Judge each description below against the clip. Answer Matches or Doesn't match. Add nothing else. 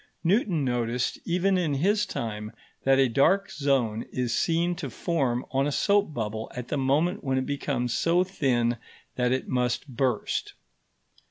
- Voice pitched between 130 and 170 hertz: Matches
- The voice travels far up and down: Matches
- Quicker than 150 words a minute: Matches